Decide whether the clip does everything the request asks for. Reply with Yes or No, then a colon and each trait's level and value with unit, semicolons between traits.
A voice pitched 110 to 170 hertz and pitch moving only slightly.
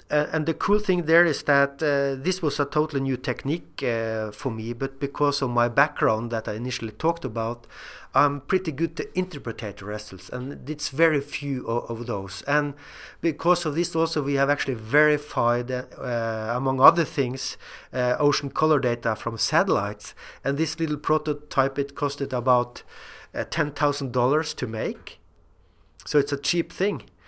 No: medium, 140 Hz; average, 4.2 semitones